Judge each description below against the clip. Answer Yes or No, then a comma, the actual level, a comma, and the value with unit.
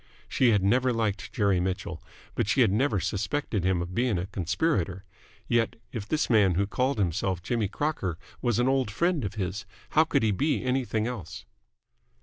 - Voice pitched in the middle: No, low, 105 Hz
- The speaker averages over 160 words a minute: Yes, average, 180 wpm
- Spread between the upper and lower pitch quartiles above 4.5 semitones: Yes, average, 5.3 semitones